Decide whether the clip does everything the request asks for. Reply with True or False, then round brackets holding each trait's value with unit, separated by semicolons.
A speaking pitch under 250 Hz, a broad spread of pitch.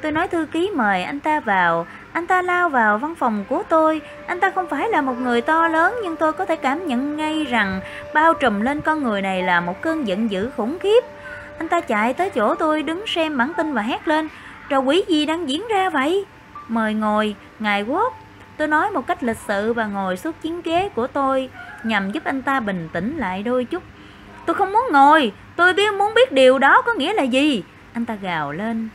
False (295 Hz; 6.5 semitones)